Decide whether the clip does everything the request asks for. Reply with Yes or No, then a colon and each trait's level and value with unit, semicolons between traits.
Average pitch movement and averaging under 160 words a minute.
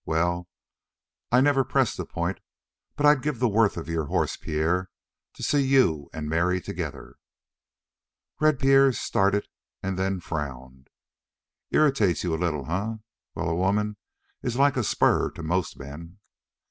No: wide, 7.5 semitones; average, 150 wpm